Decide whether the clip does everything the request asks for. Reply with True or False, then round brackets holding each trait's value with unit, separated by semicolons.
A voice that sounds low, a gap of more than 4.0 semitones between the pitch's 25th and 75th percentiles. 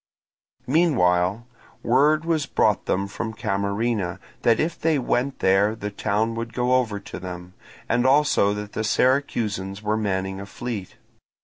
True (110 Hz; 4.4 semitones)